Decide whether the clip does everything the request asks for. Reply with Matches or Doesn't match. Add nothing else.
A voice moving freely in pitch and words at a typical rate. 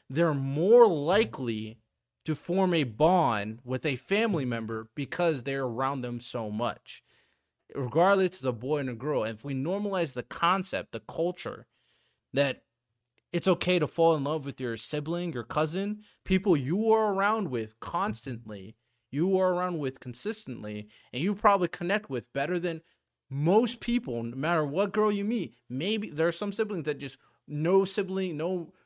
Matches